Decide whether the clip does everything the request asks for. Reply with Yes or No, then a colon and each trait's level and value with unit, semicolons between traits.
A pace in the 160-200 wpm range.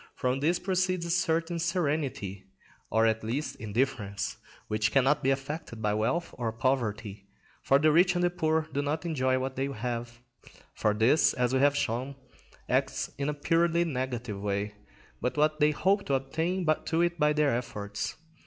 Yes: average, 170 wpm